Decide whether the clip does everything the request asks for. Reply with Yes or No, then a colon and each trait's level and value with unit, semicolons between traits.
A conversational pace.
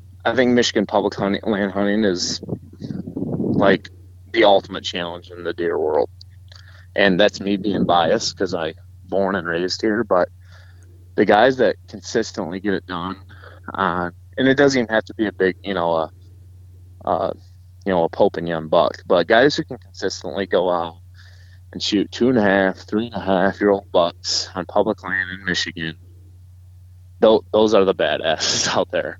Yes: average, 180 wpm